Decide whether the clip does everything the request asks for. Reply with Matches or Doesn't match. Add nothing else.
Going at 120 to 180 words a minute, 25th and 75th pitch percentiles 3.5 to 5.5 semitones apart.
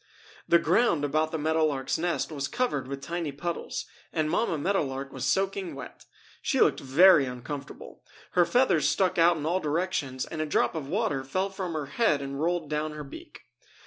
Doesn't match